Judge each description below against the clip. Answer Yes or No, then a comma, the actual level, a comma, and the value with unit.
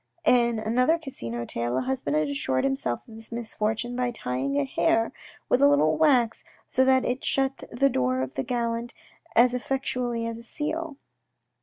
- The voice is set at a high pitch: Yes, high, 235 Hz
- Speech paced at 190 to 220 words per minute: No, average, 175 wpm